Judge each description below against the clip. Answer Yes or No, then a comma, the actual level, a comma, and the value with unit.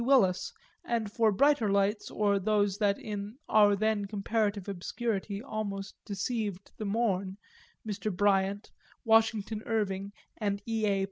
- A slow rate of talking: Yes, slow, 130 wpm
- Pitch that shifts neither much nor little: No, narrow, 1.8 semitones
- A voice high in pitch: Yes, high, 205 Hz